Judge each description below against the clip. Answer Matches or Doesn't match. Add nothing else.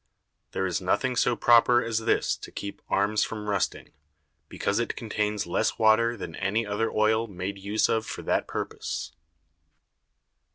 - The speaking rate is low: Doesn't match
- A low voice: Matches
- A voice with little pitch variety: Matches